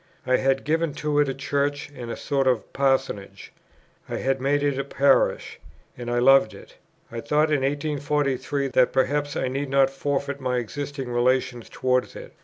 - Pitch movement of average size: No, narrow, 2.0 semitones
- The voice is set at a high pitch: No, low, 135 Hz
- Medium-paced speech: Yes, average, 180 wpm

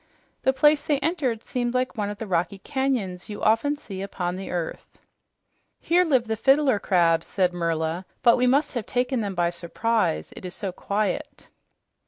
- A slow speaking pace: No, average, 180 wpm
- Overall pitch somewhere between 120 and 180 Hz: No, high, 215 Hz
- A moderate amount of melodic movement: No, wide, 6.4 semitones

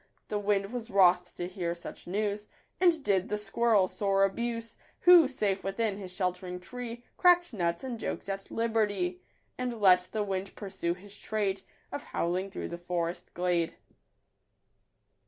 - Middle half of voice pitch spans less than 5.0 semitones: Yes, average, 3.8 semitones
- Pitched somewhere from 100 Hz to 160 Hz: No, high, 195 Hz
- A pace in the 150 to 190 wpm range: Yes, average, 155 wpm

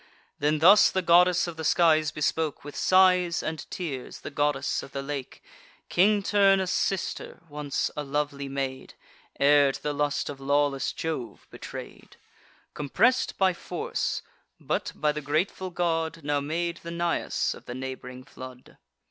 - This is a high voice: No, medium, 150 Hz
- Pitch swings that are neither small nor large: Yes, average, 3.5 semitones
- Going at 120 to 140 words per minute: No, average, 150 wpm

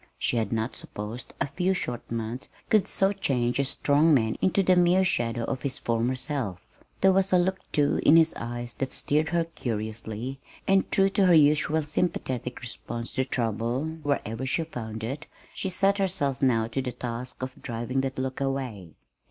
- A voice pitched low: Yes, low, 130 Hz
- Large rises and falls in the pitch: Yes, wide, 5.7 semitones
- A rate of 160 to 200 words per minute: Yes, average, 185 wpm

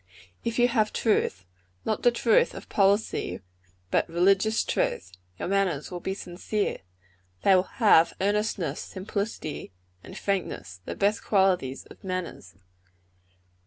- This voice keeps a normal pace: No, slow, 125 wpm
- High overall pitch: Yes, high, 195 Hz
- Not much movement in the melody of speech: No, average, 3.4 semitones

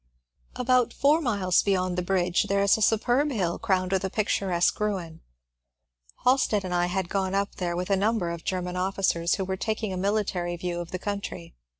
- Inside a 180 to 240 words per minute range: Yes, average, 200 wpm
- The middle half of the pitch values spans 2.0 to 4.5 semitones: Yes, average, 2.8 semitones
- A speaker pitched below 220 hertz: Yes, high, 190 Hz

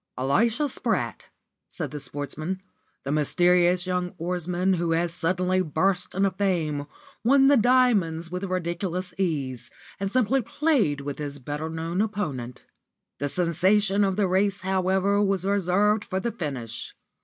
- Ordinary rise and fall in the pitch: Yes, average, 3.8 semitones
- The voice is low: No, medium, 180 Hz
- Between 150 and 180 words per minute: No, average, 140 wpm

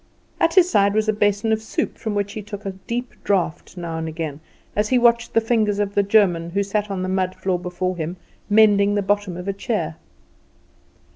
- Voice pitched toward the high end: Yes, high, 200 Hz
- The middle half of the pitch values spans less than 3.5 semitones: Yes, average, 2.7 semitones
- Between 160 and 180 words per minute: No, fast, 205 wpm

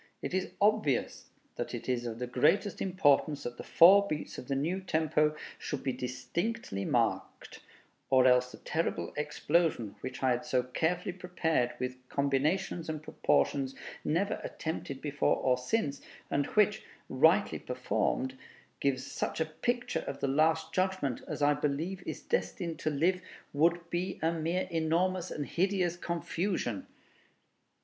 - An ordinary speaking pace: Yes, average, 150 wpm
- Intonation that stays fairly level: No, average, 5.2 semitones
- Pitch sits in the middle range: Yes, medium, 155 Hz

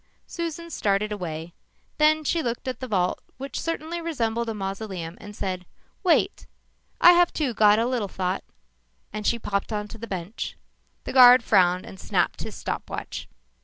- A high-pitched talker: Yes, high, 220 Hz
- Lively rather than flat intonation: Yes, wide, 6.2 semitones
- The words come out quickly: No, average, 165 wpm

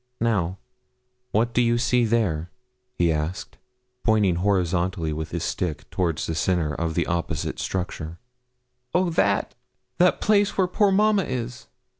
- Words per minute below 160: Yes, average, 140 wpm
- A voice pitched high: No, very low, 95 Hz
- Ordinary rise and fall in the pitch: No, wide, 6.2 semitones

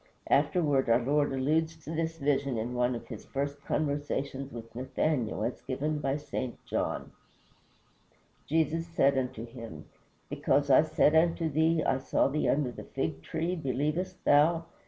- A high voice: No, medium, 140 Hz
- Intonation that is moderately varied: Yes, average, 3.5 semitones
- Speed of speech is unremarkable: Yes, average, 155 wpm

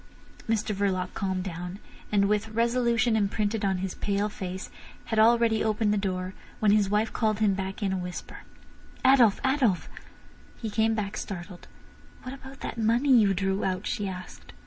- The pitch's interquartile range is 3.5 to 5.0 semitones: No, average, 2.7 semitones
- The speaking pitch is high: Yes, high, 210 Hz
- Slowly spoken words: No, average, 170 wpm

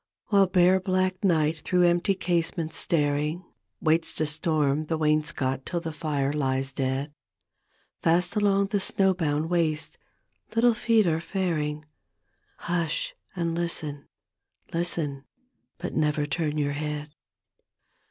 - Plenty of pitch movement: No, average, 3.1 semitones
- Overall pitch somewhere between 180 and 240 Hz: No, medium, 160 Hz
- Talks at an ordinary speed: No, slow, 130 wpm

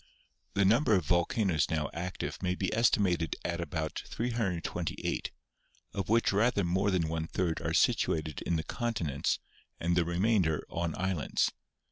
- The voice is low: Yes, very low, 90 Hz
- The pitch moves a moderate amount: Yes, average, 3.7 semitones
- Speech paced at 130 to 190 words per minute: Yes, average, 150 wpm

